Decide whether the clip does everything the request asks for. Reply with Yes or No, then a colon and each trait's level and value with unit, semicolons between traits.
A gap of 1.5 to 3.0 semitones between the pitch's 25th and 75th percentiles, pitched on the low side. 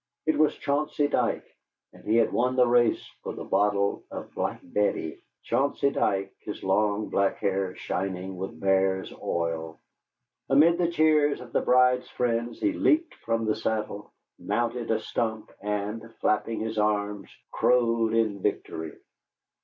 No: average, 3.9 semitones; low, 110 Hz